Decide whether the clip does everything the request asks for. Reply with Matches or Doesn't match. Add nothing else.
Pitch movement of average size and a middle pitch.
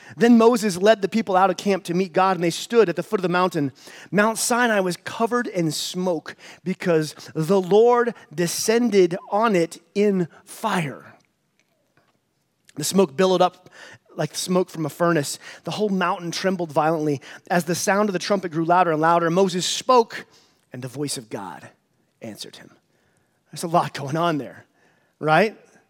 Matches